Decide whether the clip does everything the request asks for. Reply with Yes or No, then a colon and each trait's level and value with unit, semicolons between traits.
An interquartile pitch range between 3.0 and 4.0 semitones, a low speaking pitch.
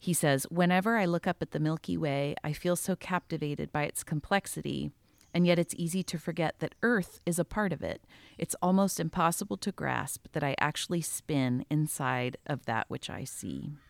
No: average, 3.4 semitones; medium, 170 Hz